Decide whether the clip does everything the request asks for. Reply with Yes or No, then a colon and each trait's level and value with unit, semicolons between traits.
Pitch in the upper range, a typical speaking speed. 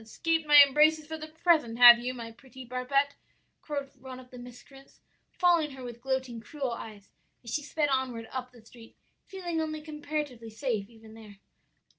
Yes: very high, 260 Hz; average, 175 wpm